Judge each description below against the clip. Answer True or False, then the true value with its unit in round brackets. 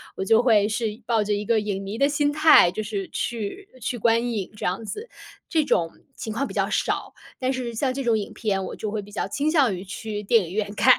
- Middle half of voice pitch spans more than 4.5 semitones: False (3.8 semitones)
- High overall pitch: True (220 Hz)